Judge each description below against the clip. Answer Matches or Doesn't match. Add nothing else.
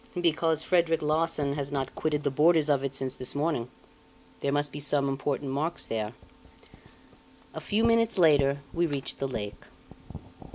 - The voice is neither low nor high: Matches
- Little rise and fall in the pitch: Doesn't match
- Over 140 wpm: Matches